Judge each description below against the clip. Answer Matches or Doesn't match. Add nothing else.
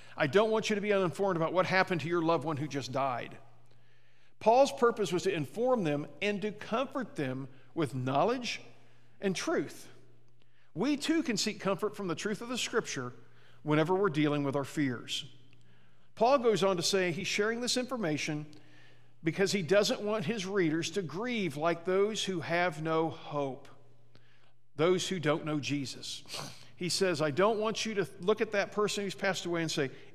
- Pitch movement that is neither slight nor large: Doesn't match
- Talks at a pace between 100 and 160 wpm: Doesn't match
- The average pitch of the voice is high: Doesn't match